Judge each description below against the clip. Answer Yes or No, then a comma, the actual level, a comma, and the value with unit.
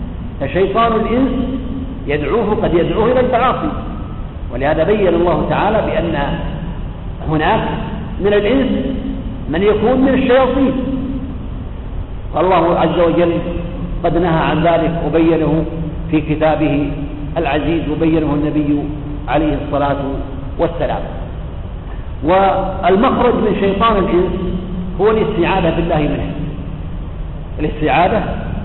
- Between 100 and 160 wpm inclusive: No, average, 90 wpm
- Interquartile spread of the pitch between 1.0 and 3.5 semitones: No, wide, 5.5 semitones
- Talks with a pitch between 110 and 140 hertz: No, medium, 165 Hz